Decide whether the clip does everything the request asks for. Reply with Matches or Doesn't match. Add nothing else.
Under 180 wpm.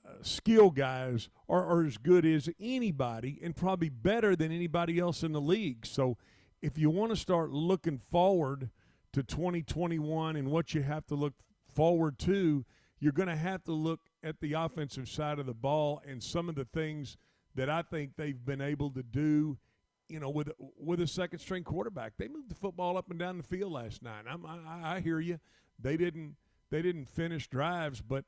Doesn't match